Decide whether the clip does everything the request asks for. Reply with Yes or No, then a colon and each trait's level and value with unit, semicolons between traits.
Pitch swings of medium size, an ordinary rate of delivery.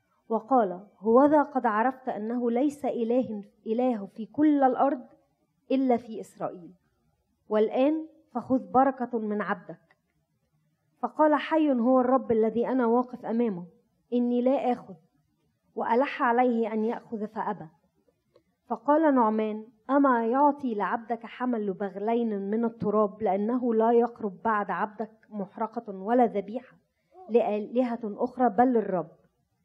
Yes: average, 3.0 semitones; average, 115 wpm